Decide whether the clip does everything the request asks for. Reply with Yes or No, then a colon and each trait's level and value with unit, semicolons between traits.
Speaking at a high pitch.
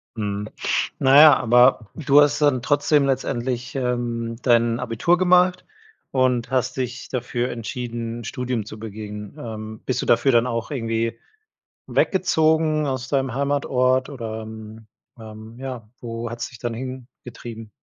No: low, 125 Hz